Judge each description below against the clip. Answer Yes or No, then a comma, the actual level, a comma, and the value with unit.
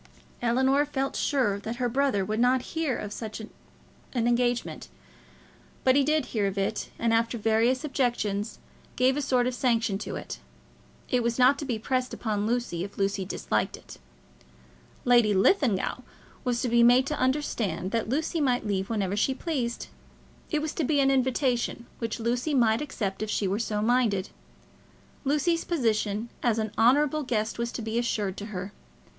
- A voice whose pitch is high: Yes, high, 235 Hz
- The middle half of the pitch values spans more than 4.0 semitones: No, average, 3.6 semitones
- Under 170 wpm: No, average, 175 wpm